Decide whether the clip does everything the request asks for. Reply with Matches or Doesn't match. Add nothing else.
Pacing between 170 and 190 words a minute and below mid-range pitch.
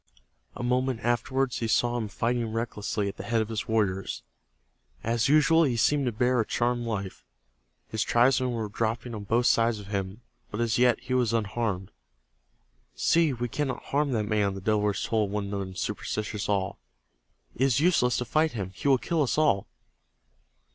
Matches